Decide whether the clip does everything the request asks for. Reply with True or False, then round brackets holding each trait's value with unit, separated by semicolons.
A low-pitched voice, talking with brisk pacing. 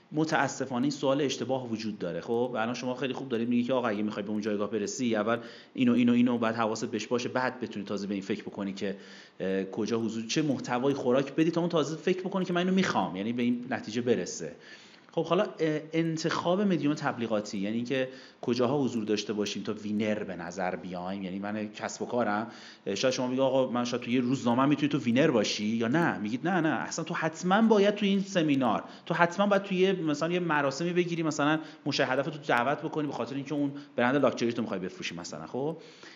True (130 Hz; 210 wpm)